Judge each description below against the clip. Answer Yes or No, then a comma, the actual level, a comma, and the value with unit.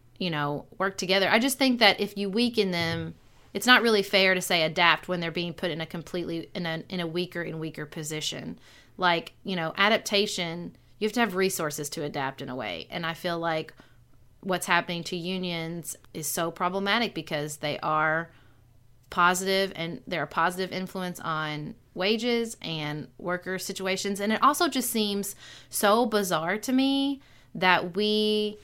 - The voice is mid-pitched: Yes, medium, 180 Hz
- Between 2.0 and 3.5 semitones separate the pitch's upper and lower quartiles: No, average, 3.9 semitones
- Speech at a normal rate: Yes, average, 175 wpm